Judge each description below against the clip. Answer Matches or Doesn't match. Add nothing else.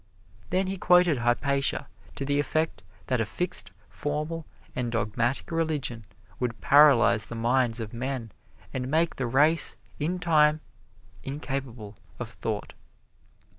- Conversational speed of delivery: Doesn't match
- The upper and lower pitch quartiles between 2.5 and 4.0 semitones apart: Doesn't match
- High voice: Doesn't match